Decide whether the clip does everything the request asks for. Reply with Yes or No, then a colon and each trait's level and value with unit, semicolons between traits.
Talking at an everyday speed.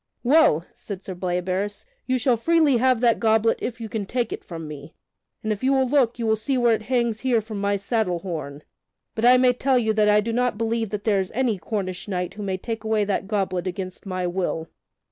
No: fast, 230 wpm